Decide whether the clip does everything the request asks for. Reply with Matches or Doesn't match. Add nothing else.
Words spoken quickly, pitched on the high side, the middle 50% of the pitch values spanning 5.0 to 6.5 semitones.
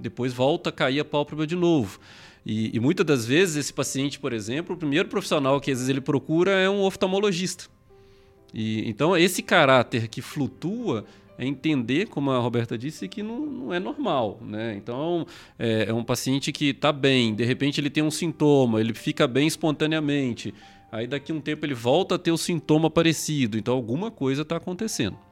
Doesn't match